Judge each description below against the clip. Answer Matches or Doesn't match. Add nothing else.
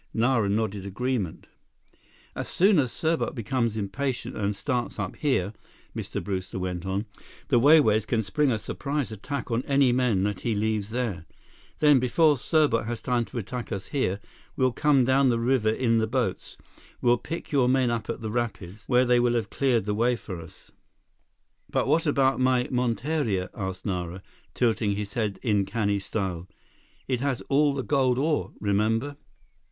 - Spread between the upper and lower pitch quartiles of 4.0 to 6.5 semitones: Matches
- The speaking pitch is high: Doesn't match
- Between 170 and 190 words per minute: Matches